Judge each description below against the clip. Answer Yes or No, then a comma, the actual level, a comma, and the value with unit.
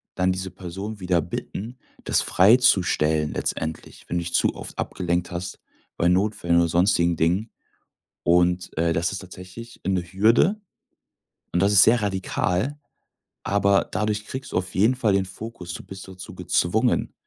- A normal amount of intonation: Yes, average, 3.2 semitones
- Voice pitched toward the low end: Yes, very low, 95 Hz